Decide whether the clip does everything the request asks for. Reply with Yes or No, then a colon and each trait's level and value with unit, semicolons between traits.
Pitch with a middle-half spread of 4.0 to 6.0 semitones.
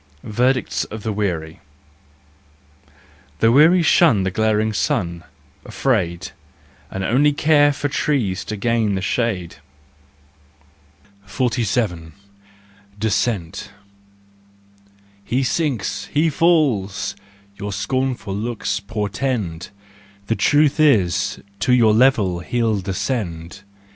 Yes: average, 4.9 semitones